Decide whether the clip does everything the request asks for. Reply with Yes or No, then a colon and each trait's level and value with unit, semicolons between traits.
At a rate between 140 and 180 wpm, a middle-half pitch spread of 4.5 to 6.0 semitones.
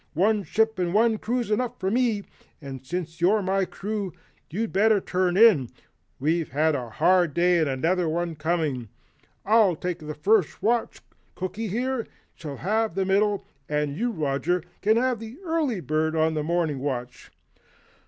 Yes: average, 155 wpm; wide, 5.5 semitones